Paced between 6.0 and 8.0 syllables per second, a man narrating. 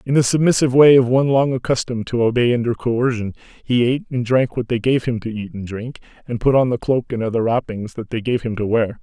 Yes: 6.1 syllables/s; male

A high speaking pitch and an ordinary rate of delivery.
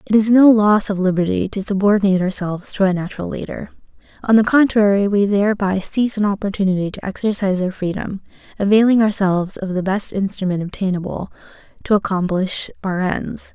Yes: high, 200 Hz; average, 160 wpm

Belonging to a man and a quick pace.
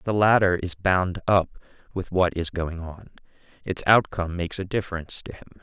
No: male; average, 180 wpm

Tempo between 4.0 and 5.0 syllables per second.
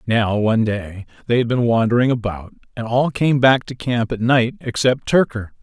Yes: 4.9 syllables/s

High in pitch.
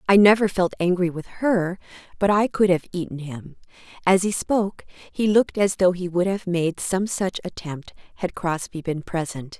No: medium, 180 Hz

